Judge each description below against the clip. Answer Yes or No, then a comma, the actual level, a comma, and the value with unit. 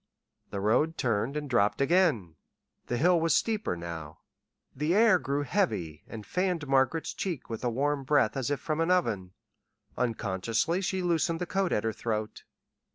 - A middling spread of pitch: No, wide, 7.4 semitones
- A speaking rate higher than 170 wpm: No, average, 165 wpm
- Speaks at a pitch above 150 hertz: No, medium, 140 Hz